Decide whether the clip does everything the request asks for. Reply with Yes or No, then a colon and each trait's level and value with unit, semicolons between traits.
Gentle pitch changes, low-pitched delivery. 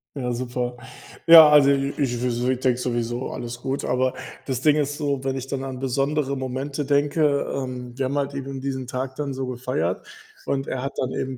Yes: narrow, 1.7 semitones; low, 130 Hz